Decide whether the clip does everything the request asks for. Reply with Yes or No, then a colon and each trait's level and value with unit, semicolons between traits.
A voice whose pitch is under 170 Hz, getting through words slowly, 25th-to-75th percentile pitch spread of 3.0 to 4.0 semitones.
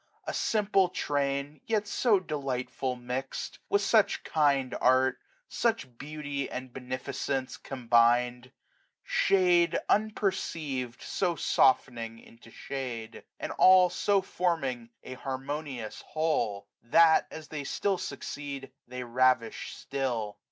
No: low, 135 Hz; slow, 110 wpm; average, 4.9 semitones